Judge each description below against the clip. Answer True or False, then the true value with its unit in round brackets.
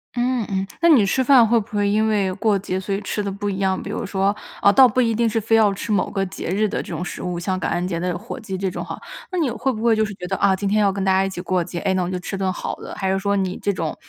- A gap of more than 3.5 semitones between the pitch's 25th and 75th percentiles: False (2.5 semitones)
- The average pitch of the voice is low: False (200 Hz)